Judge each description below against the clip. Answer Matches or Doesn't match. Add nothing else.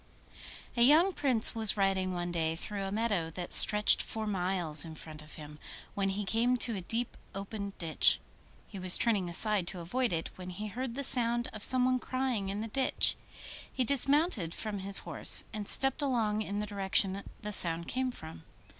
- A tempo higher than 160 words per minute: Matches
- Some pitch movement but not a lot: Matches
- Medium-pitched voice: Doesn't match